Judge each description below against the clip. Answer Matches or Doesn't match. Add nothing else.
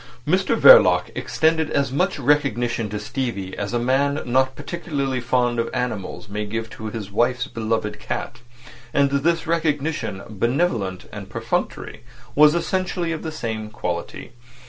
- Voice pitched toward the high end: Doesn't match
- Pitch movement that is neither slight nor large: Doesn't match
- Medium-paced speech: Matches